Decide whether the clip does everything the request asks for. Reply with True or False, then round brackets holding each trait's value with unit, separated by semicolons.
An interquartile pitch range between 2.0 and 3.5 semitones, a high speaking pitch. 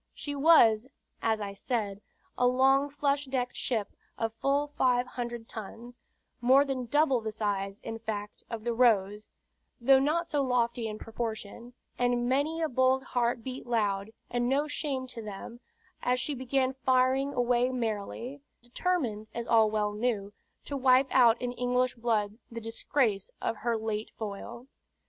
True (2.9 semitones; 245 Hz)